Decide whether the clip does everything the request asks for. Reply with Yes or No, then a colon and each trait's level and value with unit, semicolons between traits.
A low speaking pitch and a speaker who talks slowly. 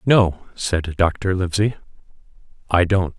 Yes: very low, 95 Hz; slow, 115 wpm